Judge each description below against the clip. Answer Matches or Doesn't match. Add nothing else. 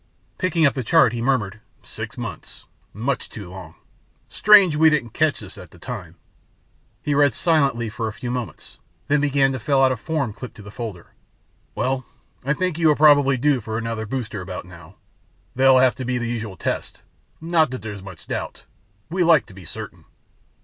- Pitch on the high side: Doesn't match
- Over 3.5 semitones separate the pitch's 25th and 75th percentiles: Matches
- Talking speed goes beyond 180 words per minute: Matches